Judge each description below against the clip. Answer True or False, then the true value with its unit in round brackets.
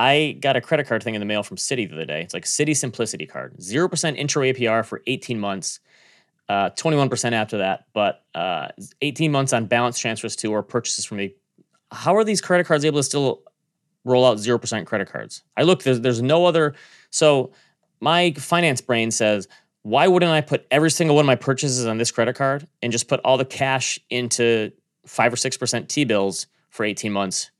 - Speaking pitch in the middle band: False (125 Hz)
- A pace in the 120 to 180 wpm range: False (205 wpm)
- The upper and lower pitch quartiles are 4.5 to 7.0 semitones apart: True (4.9 semitones)